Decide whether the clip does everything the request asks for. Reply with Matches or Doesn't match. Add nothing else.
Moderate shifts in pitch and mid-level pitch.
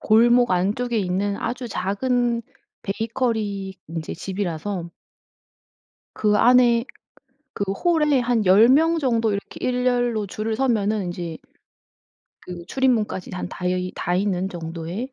Doesn't match